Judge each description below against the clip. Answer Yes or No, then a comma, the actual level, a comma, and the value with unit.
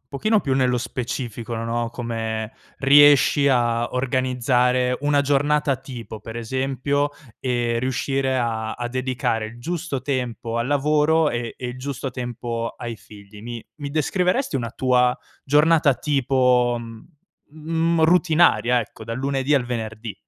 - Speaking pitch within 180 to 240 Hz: No, low, 125 Hz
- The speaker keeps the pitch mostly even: No, average, 3.3 semitones